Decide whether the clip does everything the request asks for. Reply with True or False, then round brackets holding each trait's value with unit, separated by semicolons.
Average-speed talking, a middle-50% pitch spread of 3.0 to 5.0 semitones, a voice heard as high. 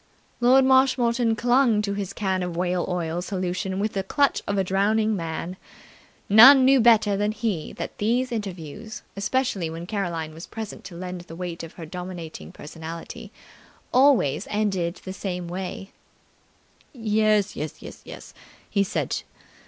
True (150 wpm; 3.8 semitones; 195 Hz)